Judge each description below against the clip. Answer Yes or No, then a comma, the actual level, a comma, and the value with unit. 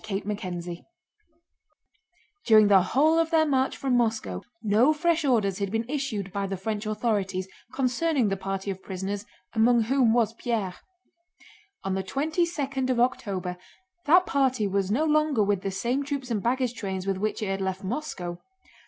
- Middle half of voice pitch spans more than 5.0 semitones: Yes, wide, 5.5 semitones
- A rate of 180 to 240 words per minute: No, average, 170 wpm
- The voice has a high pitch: Yes, high, 220 Hz